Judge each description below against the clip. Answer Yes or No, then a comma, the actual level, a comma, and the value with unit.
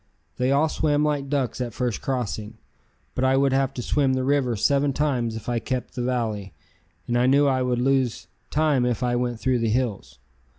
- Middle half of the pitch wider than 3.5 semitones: No, narrow, 2.4 semitones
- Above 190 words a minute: Yes, average, 200 wpm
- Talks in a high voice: No, low, 125 Hz